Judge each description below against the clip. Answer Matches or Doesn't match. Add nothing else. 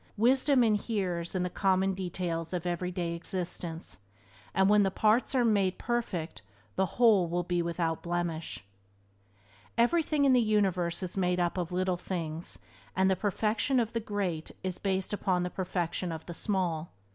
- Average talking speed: Matches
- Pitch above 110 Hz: Matches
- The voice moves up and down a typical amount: Matches